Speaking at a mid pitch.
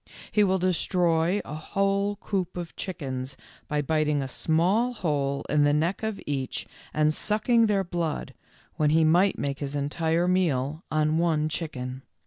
Yes: medium, 160 Hz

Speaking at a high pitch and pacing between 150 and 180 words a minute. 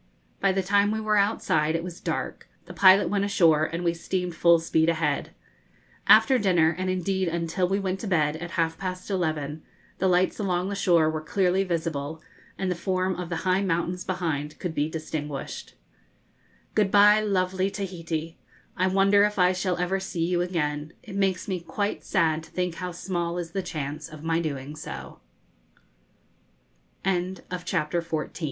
No: medium, 180 Hz; average, 170 wpm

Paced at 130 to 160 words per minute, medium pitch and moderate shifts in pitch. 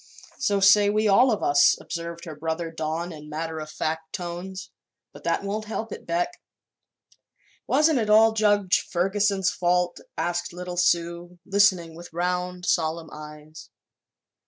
Yes: average, 145 wpm; medium, 175 Hz; average, 3.5 semitones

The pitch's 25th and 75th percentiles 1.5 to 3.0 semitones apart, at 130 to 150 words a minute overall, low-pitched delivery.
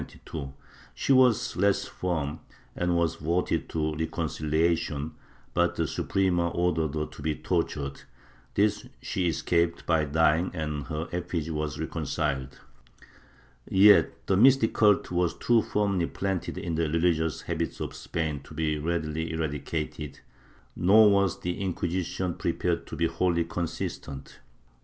Yes: average, 2.7 semitones; slow, 135 wpm; very low, 85 Hz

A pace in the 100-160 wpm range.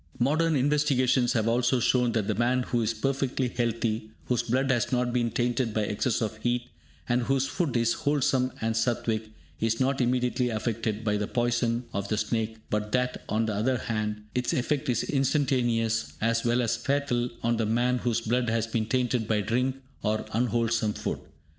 No: average, 185 wpm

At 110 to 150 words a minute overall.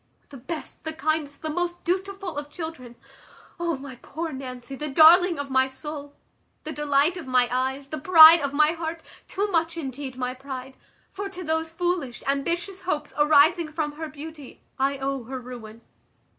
No: average, 170 wpm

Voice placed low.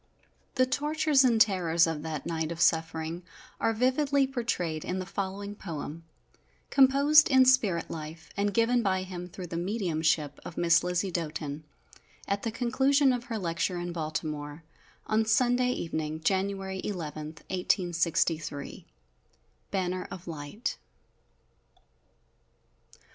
No: medium, 185 Hz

